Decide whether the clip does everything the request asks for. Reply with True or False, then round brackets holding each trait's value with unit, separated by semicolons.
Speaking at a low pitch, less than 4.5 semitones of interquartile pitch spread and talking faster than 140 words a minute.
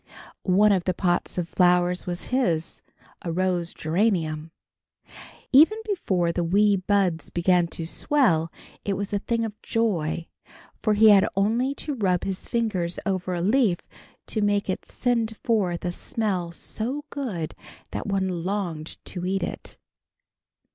False (190 Hz; 3.9 semitones; 150 wpm)